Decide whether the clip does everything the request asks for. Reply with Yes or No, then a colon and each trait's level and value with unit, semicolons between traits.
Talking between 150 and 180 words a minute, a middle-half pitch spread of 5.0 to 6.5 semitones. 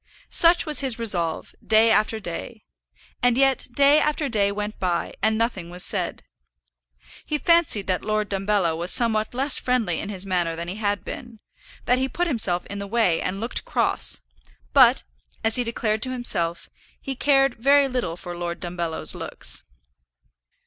Yes: average, 170 wpm; wide, 5.6 semitones